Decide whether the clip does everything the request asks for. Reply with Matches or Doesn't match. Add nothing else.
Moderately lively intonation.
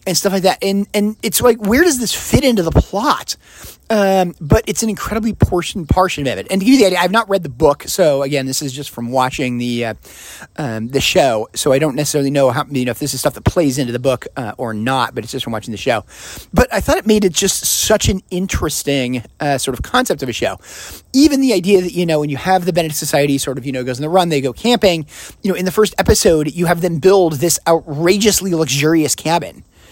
Doesn't match